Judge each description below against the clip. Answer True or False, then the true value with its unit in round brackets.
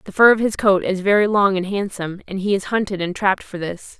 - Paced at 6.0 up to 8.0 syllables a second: True (6.1 syllables/s)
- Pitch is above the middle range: True (195 Hz)